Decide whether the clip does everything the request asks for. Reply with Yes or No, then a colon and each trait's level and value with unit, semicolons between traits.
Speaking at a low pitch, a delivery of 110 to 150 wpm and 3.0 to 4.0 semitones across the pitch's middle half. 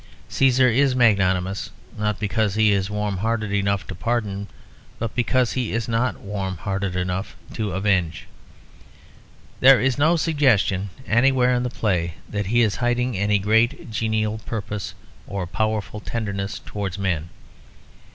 Yes: low, 105 Hz; average, 140 wpm; average, 3.4 semitones